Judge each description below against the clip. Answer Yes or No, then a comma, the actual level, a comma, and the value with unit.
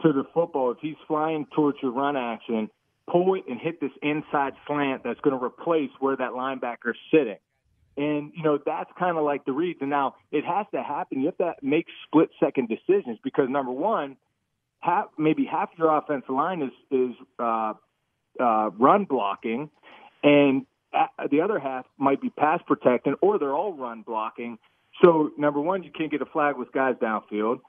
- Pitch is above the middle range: No, medium, 140 Hz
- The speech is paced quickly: No, average, 175 wpm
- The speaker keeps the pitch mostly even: No, average, 3.5 semitones